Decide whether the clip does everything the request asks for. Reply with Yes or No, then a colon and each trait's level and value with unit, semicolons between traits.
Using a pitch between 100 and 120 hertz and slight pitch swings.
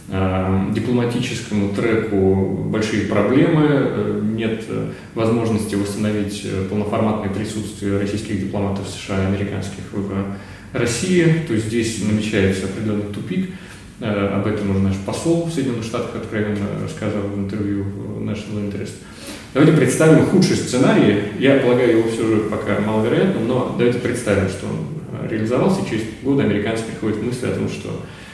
Yes: low, 105 Hz; narrow, 2.3 semitones